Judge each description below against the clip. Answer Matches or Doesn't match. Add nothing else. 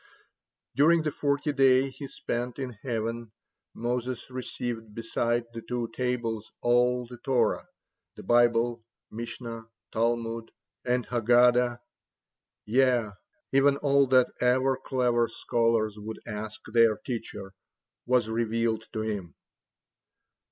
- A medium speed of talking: Doesn't match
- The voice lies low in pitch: Matches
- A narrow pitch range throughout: Matches